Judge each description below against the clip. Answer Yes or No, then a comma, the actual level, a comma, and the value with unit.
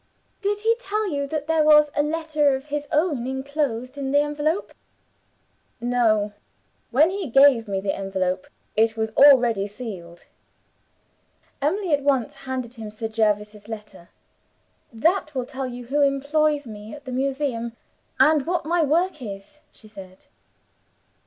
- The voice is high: Yes, very high, 270 Hz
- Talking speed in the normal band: Yes, average, 150 wpm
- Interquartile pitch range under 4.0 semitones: No, average, 5.3 semitones